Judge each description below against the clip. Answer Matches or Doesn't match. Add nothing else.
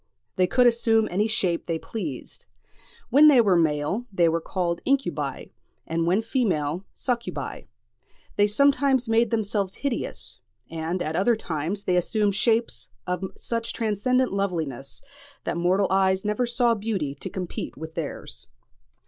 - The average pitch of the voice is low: Doesn't match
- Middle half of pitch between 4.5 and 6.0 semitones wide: Matches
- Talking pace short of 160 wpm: Matches